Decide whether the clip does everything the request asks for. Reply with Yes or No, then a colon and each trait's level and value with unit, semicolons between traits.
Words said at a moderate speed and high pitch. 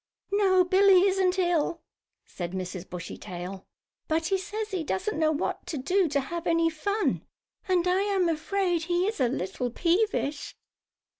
Yes: average, 155 wpm; very high, 345 Hz